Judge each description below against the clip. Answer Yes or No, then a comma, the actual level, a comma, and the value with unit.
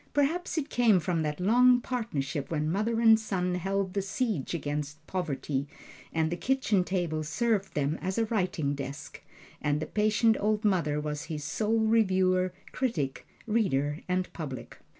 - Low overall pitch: No, medium, 185 Hz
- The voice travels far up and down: Yes, wide, 6.4 semitones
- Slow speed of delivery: No, average, 155 wpm